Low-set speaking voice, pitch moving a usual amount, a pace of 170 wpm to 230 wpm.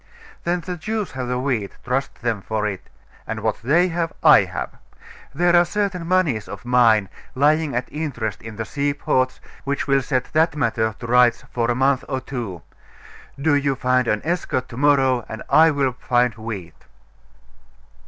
Yes: low, 130 Hz; average, 4.6 semitones; average, 175 wpm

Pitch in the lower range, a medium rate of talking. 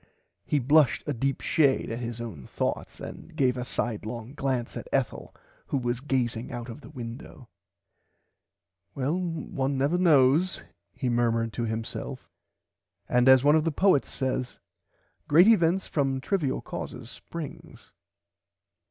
Yes: low, 130 Hz; average, 145 wpm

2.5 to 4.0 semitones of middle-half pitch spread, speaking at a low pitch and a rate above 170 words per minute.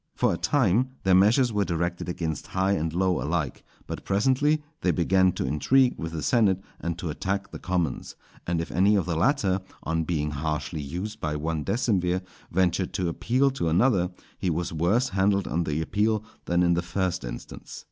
Yes: average, 3.7 semitones; very low, 90 Hz; average, 190 wpm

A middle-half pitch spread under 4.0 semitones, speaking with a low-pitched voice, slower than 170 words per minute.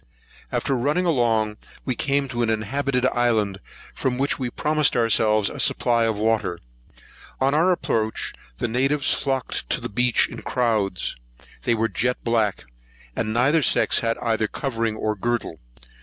Yes: average, 3.4 semitones; low, 120 Hz; average, 155 wpm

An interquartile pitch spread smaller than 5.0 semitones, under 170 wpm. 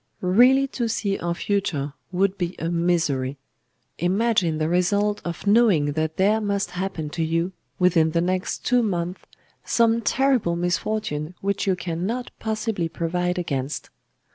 Yes: average, 3.8 semitones; average, 140 wpm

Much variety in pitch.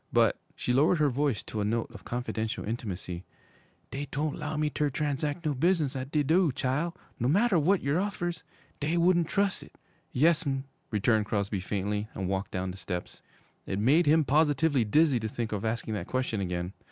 Yes: wide, 6.4 semitones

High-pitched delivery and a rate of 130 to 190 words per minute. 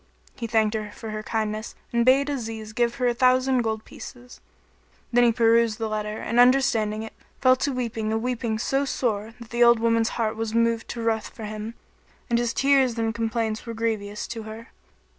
No: high, 230 Hz; average, 200 wpm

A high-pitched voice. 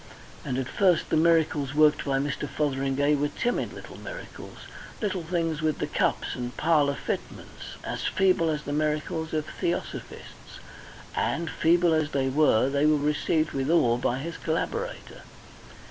No: medium, 155 Hz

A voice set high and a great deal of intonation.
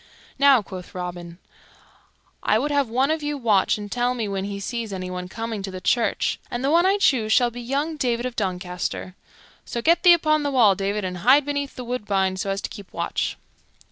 Yes: high, 230 Hz; wide, 5.9 semitones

